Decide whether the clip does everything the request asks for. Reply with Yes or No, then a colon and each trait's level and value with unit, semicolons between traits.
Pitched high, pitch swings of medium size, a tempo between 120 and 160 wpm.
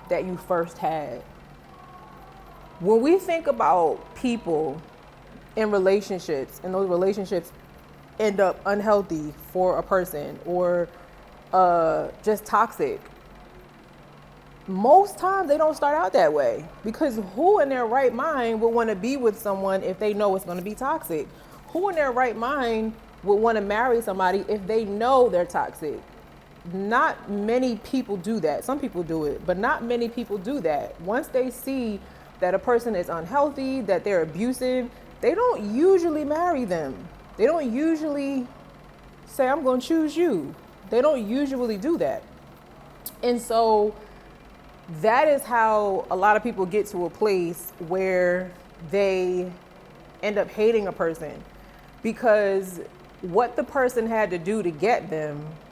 No: high, 215 Hz; wide, 5.8 semitones; average, 150 wpm